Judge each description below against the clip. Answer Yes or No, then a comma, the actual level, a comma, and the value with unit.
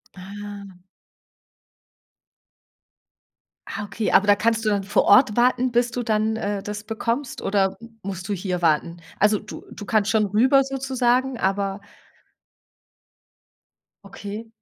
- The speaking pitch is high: Yes, high, 210 Hz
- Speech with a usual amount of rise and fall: Yes, average, 3.0 semitones